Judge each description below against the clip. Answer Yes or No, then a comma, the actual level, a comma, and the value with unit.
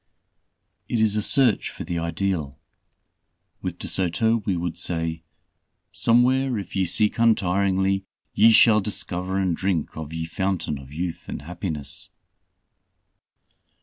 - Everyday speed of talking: No, slow, 130 wpm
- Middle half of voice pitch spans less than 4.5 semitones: Yes, average, 4.1 semitones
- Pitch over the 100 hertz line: No, very low, 95 Hz